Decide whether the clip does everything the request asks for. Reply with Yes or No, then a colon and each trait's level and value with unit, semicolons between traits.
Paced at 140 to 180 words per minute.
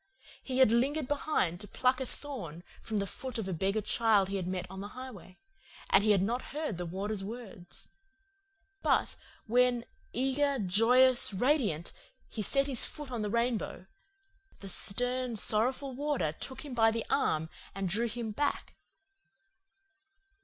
Yes: average, 160 wpm